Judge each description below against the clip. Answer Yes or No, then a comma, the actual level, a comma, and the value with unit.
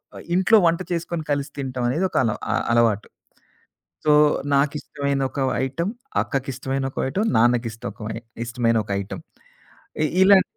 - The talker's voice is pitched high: No, low, 135 Hz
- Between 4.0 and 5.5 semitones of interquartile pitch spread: Yes, average, 5.2 semitones